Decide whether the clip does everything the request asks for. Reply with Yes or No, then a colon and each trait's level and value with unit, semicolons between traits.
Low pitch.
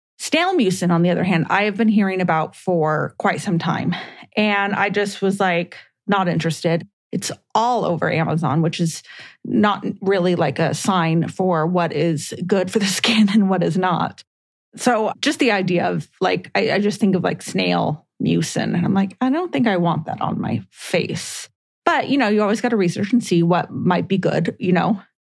No: high, 190 Hz